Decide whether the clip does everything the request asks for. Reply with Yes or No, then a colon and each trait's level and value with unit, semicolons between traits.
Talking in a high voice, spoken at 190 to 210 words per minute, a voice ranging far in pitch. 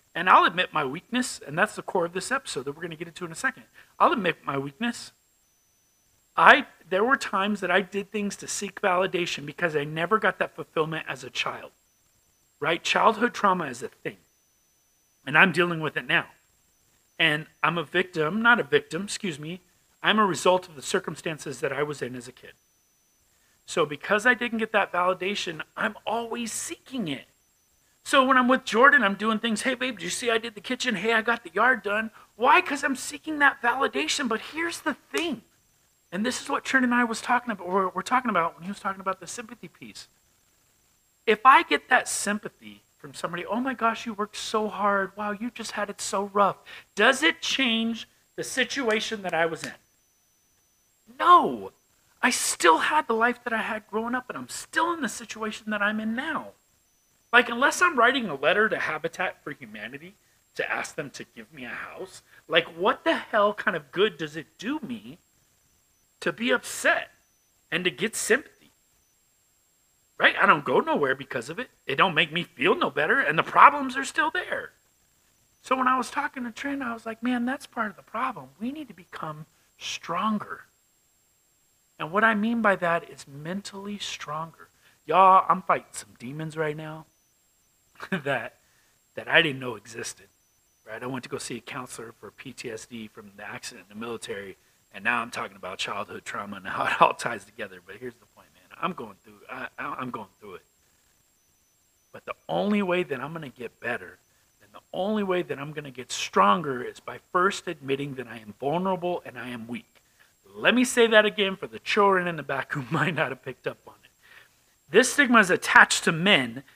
Yes: high, 200 Hz; average, 200 wpm; wide, 6.5 semitones